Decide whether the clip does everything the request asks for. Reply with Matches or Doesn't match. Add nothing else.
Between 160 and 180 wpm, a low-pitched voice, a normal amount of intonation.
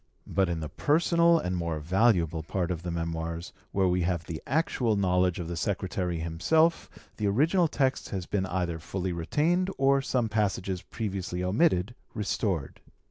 Doesn't match